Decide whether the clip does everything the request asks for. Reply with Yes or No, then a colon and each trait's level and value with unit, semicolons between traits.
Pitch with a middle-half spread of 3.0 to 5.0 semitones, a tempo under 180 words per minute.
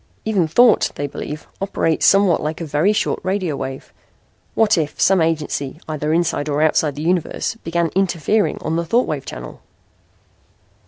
Yes: average, 4.0 semitones; average, 160 wpm